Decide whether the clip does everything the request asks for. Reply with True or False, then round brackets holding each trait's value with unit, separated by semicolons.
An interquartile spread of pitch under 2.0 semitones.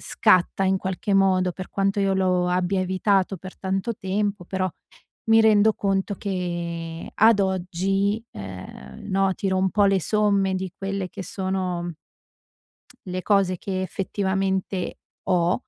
True (1.4 semitones)